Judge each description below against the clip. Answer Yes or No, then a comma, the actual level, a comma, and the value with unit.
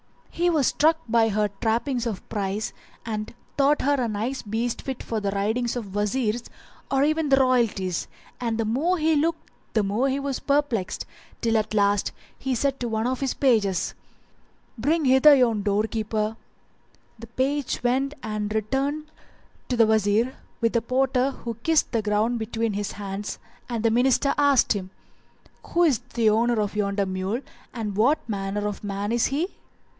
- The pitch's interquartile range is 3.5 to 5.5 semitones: Yes, average, 4.2 semitones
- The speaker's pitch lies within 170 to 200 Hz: No, high, 230 Hz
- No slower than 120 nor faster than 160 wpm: No, average, 170 wpm